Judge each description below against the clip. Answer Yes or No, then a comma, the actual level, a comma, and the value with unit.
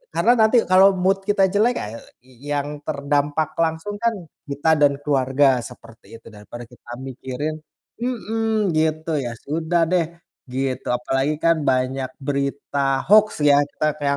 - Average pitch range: Yes, average, 4.7 semitones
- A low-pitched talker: No, medium, 145 Hz